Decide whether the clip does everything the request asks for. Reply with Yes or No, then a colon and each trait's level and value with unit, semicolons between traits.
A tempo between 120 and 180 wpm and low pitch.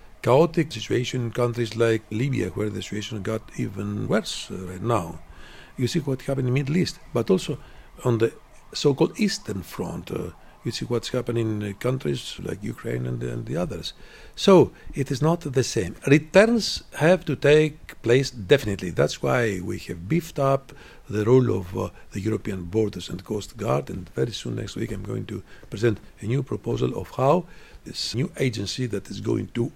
No: average, 190 wpm; low, 120 Hz